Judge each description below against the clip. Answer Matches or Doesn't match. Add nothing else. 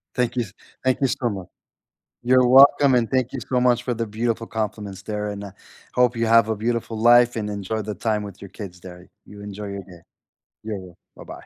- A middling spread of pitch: Matches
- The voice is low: Matches